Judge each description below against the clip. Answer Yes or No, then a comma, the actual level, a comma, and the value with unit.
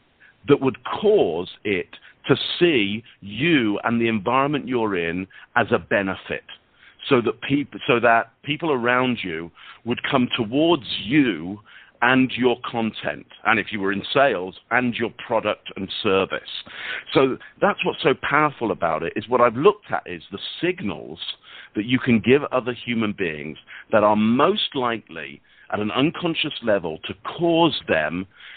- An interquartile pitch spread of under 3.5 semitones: No, average, 4.7 semitones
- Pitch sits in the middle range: No, low, 120 Hz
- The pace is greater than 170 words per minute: No, average, 165 wpm